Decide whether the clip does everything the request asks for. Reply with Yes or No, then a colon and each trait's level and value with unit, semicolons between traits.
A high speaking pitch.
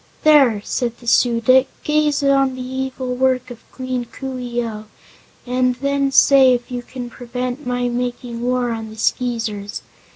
Yes: very high, 250 Hz